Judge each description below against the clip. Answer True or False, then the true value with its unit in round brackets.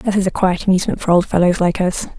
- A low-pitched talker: False (185 Hz)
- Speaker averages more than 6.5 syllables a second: True (6.8 syllables/s)